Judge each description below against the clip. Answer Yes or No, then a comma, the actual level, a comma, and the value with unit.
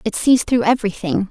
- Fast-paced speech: No, average, 185 wpm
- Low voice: No, high, 220 Hz